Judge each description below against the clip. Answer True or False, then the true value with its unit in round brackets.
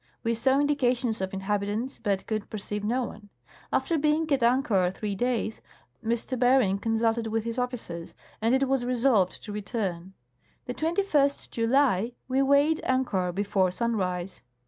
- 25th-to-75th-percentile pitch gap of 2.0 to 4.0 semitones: False (4.5 semitones)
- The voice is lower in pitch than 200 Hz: False (230 Hz)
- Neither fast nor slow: True (150 wpm)